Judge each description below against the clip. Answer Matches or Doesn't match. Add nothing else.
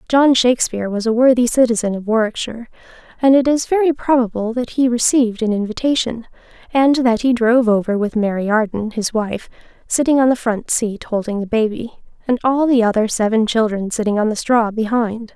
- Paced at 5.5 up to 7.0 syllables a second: Matches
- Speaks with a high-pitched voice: Matches